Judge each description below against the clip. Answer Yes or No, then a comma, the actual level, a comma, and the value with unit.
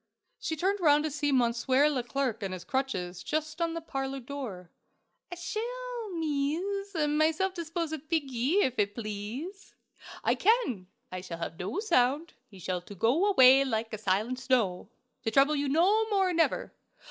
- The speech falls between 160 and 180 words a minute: Yes, average, 165 wpm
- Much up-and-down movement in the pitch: Yes, wide, 6.5 semitones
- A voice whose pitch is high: Yes, very high, 280 Hz